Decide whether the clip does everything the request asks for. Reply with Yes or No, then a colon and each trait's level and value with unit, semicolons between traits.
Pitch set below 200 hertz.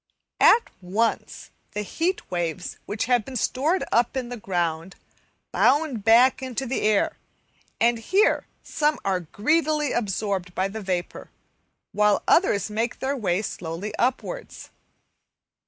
No: high, 225 Hz